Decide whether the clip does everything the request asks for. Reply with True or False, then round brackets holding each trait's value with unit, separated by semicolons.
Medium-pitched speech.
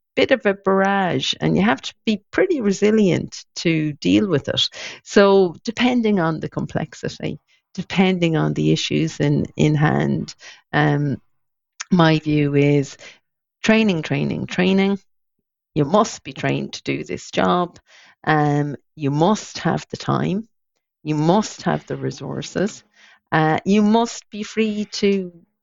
True (180 Hz)